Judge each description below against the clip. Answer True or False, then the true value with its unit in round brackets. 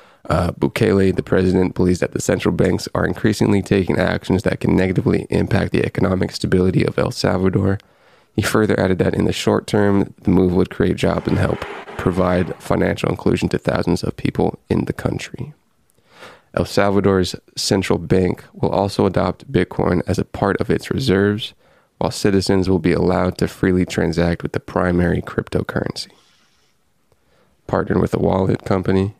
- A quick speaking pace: False (160 wpm)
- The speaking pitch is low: True (95 Hz)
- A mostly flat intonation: True (1.7 semitones)